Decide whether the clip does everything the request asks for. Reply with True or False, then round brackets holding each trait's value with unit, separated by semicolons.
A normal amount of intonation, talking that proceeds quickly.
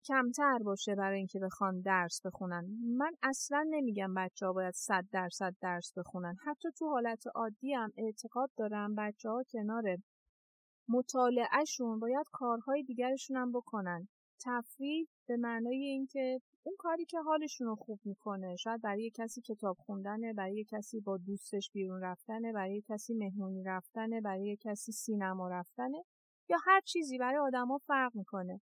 False (4.9 semitones; 145 wpm)